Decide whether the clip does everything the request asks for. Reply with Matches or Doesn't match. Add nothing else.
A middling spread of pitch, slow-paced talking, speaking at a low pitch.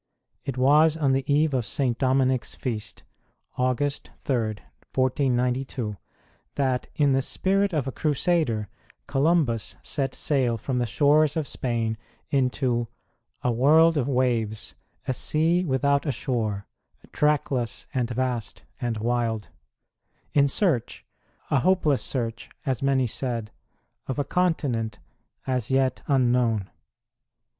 Matches